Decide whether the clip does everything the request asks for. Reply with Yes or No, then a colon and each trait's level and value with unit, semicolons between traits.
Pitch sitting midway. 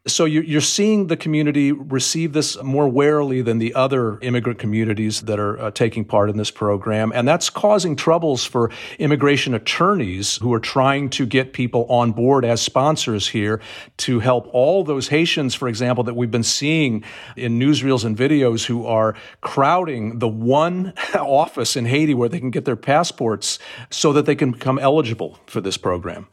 No: low, 125 Hz